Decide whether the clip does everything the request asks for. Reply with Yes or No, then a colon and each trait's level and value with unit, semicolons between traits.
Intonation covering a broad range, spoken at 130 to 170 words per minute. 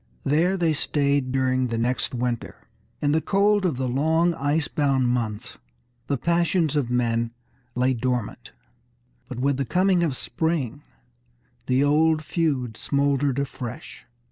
No: average, 4.2 semitones; average, 140 wpm